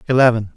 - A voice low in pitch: Yes, low, 110 Hz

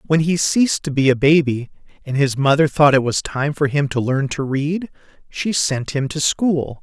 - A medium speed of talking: No, fast, 220 wpm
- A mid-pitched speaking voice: Yes, medium, 145 Hz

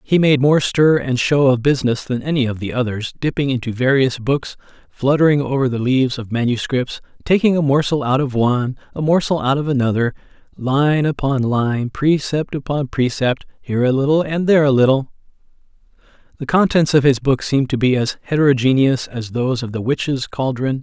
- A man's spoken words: Yes, male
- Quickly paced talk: No, average, 185 wpm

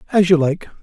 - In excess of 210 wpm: Yes, fast, 220 wpm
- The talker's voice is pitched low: No, medium, 165 Hz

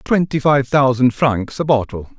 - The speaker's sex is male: Yes, male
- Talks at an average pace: Yes, average, 165 wpm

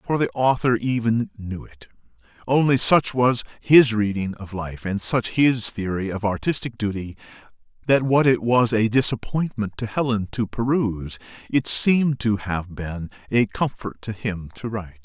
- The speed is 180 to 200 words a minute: No, average, 165 wpm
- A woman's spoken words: No, male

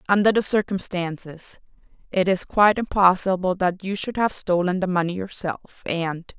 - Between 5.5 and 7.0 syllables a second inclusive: No, 5.0 syllables/s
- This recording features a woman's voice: Yes, female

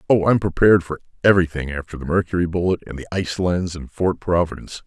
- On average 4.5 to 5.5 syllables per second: No, 6.7 syllables/s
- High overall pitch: No, very low, 85 Hz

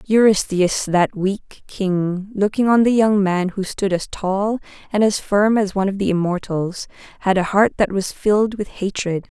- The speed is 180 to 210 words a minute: Yes, average, 185 wpm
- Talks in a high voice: Yes, high, 200 Hz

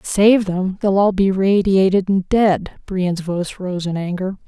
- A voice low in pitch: No, high, 190 Hz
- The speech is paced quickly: No, average, 160 wpm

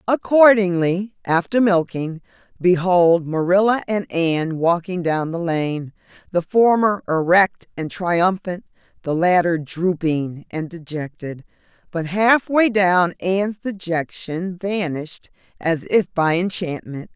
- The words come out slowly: Yes, slow, 110 wpm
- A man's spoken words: No, female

